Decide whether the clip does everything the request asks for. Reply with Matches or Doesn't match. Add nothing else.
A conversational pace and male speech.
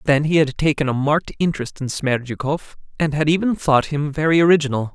Matches